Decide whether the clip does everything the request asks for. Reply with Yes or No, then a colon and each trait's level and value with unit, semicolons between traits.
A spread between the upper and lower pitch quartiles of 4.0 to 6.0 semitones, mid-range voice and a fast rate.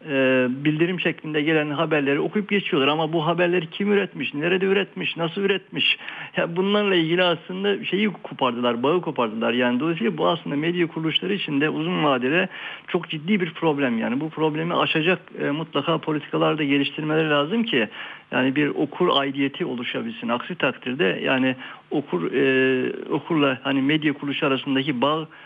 Yes: average, 4.3 semitones; medium, 155 Hz; fast, 155 wpm